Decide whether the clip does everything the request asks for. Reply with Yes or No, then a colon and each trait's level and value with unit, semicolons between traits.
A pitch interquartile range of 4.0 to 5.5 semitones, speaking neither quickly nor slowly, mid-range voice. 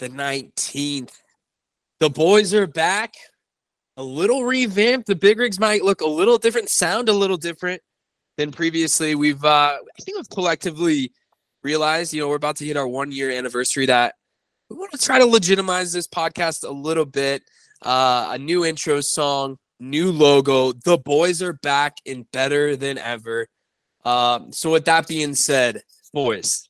Yes: average, 4.6 semitones; average, 165 wpm; medium, 155 Hz